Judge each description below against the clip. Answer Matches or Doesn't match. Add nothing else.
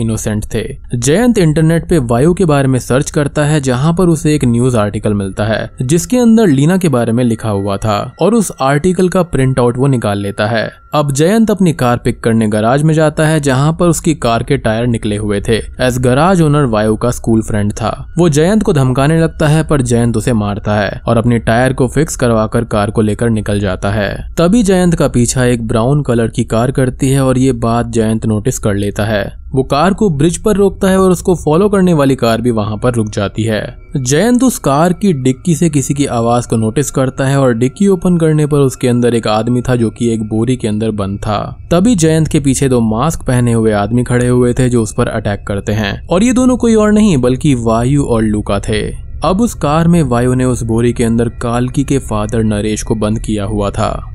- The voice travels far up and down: Matches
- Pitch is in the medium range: Doesn't match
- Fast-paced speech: Matches